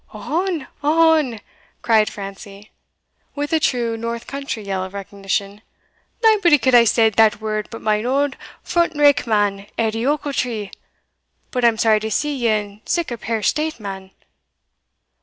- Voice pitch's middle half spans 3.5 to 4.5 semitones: No, average, 5.3 semitones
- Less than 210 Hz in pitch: No, high, 230 Hz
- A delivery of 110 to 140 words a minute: No, average, 155 wpm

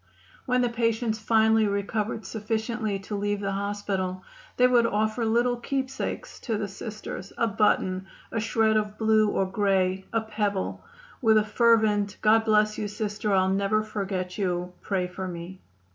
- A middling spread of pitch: No, narrow, 2.2 semitones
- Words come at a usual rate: Yes, average, 160 wpm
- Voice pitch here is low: No, high, 210 Hz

